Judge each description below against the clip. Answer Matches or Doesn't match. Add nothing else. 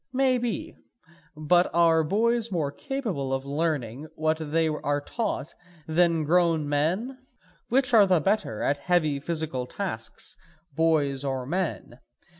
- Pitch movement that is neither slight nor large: Matches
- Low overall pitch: Doesn't match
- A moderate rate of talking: Doesn't match